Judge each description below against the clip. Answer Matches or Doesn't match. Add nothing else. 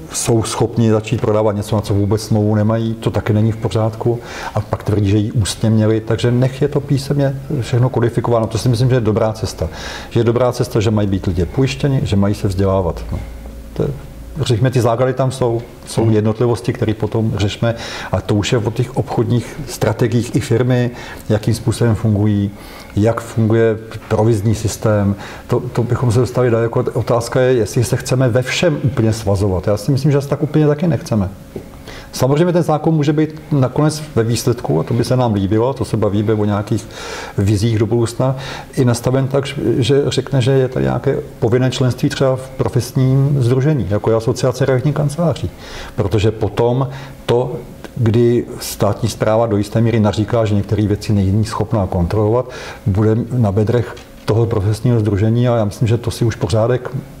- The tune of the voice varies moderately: Matches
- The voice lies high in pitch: Doesn't match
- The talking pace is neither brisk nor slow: Doesn't match